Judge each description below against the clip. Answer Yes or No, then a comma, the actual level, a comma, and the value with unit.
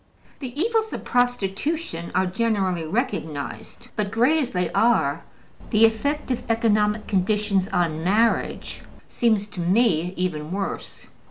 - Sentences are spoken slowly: Yes, slow, 125 wpm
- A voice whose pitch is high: Yes, high, 210 Hz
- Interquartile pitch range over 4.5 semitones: Yes, average, 4.9 semitones